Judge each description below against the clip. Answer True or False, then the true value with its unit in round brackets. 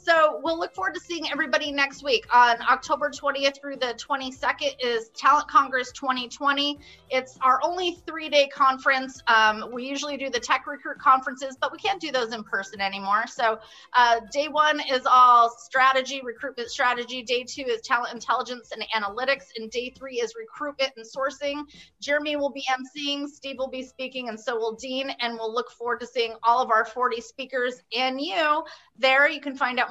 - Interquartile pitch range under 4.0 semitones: True (3.1 semitones)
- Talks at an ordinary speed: True (185 wpm)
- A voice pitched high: True (265 Hz)